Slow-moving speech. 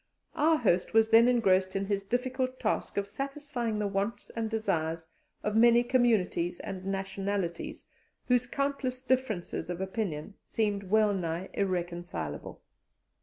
Yes: slow, 125 wpm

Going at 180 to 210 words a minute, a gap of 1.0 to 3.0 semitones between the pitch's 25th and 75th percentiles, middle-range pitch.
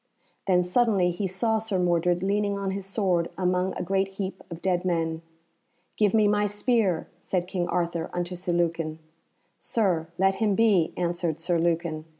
No: average, 165 wpm; narrow, 2.5 semitones; medium, 180 Hz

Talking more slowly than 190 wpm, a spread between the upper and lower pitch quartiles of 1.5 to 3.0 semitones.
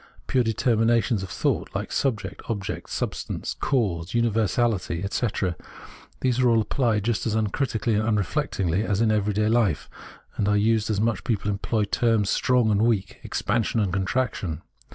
Yes: average, 165 wpm; average, 2.7 semitones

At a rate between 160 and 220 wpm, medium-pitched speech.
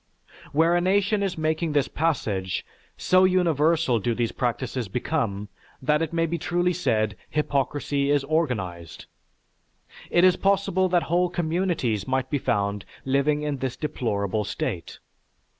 No: average, 140 wpm; medium, 150 Hz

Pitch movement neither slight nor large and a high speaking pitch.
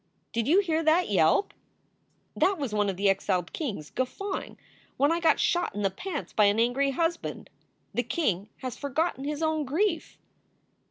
No: wide, 7.9 semitones; very high, 280 Hz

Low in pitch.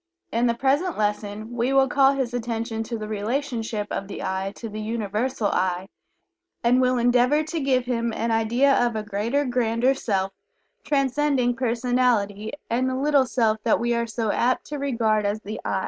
No: high, 235 Hz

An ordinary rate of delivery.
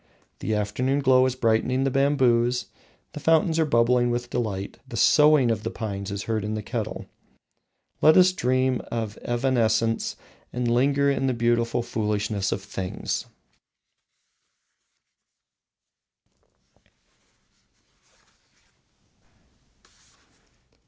No: slow, 105 wpm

